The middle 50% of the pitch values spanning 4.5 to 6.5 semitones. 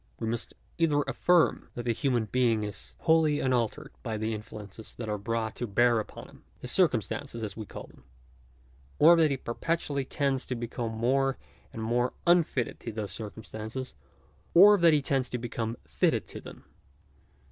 No: average, 4.0 semitones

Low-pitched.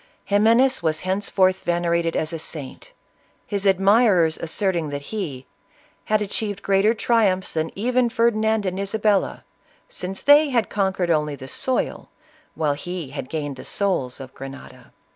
No: high, 190 Hz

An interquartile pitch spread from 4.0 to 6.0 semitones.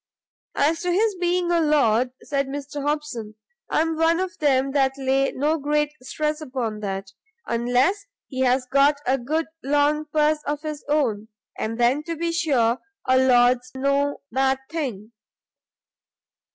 No: average, 3.3 semitones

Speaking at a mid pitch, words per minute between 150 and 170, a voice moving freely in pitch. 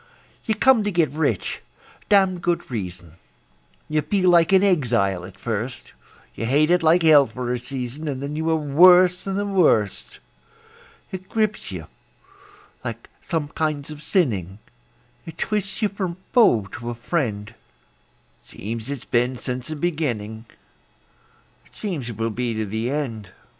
Yes: medium, 145 Hz; average, 160 wpm; wide, 7.4 semitones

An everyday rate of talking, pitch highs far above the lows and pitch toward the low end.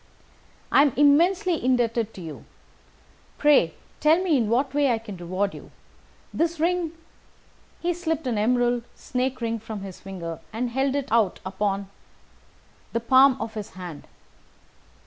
No: average, 150 wpm; wide, 5.7 semitones; high, 245 Hz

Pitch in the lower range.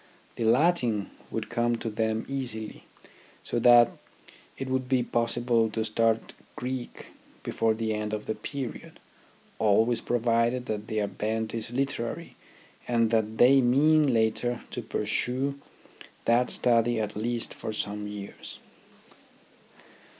Yes: low, 115 Hz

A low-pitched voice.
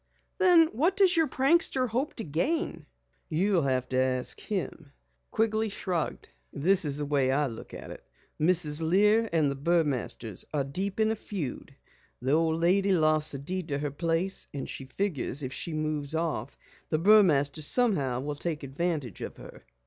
No: medium, 160 Hz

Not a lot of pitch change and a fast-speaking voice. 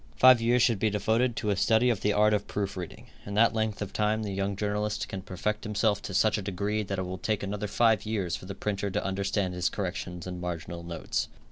Yes: narrow, 2.2 semitones; fast, 240 wpm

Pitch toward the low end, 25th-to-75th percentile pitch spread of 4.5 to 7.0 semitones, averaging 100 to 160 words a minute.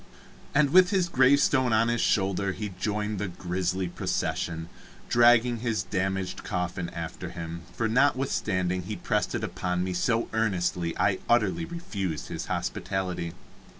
Yes: low, 100 Hz; average, 4.8 semitones; average, 140 wpm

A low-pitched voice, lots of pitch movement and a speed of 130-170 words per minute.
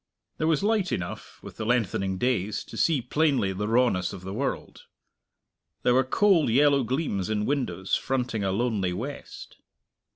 Yes: low, 120 Hz; wide, 6.2 semitones; average, 160 wpm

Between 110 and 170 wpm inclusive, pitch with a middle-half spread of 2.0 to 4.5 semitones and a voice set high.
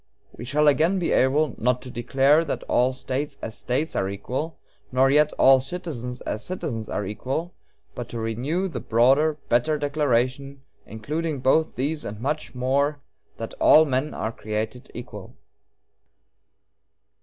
No: average, 150 wpm; average, 3.9 semitones; low, 135 Hz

